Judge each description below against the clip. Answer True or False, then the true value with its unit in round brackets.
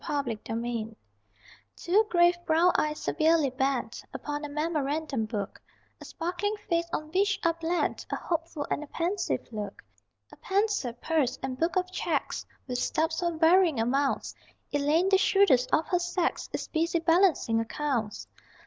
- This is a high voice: True (320 Hz)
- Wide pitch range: False (4.6 semitones)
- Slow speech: False (155 wpm)